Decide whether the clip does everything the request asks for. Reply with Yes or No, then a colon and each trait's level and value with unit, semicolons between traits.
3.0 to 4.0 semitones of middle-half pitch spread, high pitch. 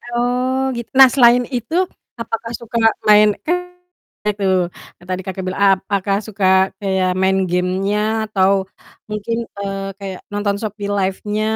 Yes: average, 3.3 semitones; high, 205 Hz